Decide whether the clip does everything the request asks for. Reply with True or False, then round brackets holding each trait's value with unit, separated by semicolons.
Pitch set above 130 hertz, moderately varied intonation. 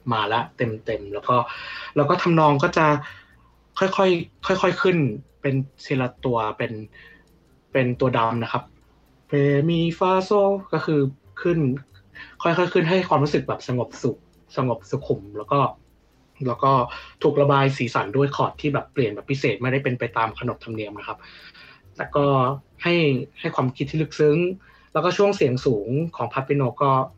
True (140 Hz; 5.0 semitones)